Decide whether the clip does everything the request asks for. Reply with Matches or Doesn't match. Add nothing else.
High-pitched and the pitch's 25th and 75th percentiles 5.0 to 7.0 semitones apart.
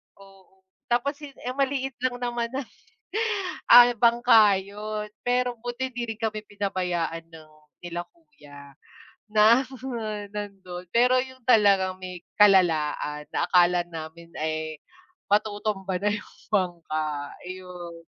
Matches